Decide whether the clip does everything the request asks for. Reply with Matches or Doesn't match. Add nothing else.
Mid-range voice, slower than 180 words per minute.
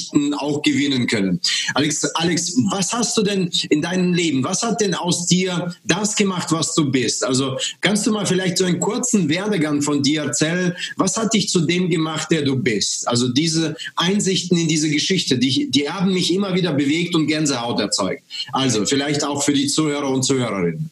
Doesn't match